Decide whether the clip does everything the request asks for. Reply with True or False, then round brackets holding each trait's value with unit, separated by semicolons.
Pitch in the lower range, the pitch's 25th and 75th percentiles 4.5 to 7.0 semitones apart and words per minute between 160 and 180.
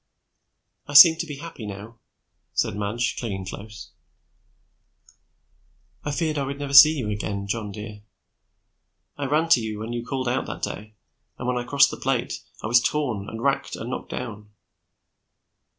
True (120 Hz; 4.8 semitones; 165 wpm)